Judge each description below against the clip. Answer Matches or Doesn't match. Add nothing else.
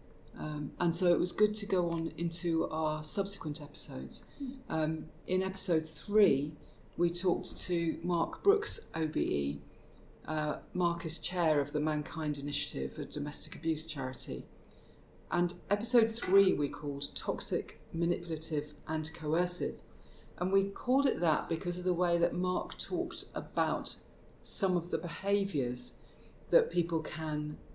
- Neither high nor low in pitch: Matches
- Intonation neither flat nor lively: Matches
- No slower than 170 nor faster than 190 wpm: Doesn't match